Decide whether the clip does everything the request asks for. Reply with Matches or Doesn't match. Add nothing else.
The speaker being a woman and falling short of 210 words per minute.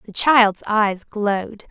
Matches